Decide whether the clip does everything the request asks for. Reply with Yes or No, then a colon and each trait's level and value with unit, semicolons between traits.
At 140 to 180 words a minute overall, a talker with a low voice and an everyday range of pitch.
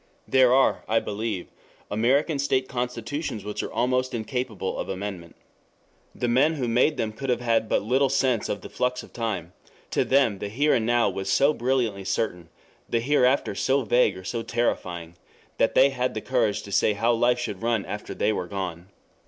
No: average, 190 wpm; low, 115 Hz; average, 3.9 semitones